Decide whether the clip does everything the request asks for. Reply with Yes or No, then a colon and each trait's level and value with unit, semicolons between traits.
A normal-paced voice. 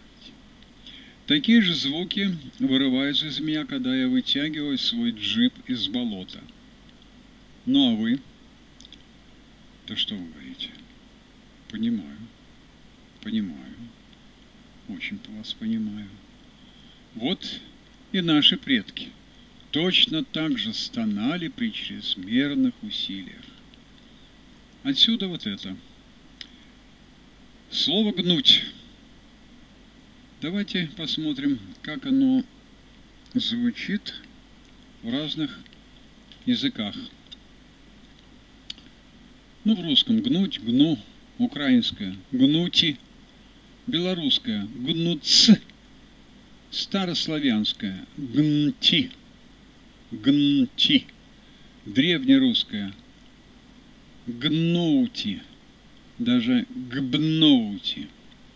No: slow, 70 wpm